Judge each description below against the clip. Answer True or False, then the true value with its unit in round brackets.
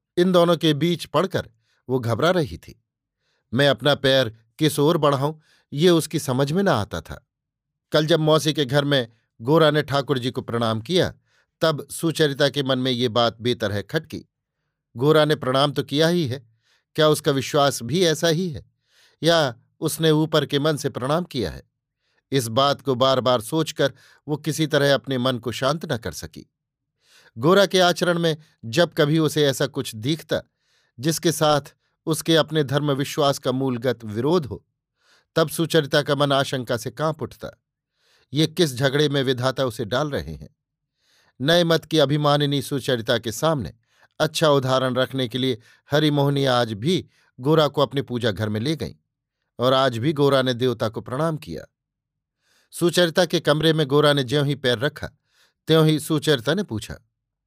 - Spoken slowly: False (175 wpm)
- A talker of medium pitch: True (145 Hz)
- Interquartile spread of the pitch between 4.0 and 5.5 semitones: False (3.5 semitones)